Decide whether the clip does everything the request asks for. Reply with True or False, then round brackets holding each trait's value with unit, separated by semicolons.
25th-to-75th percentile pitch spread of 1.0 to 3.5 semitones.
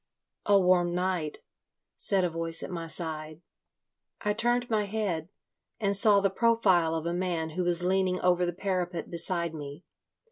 True (3.0 semitones)